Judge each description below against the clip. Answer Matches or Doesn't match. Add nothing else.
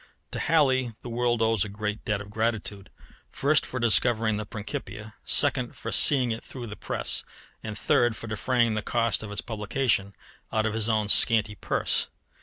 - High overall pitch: Doesn't match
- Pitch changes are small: Matches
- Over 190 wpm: Doesn't match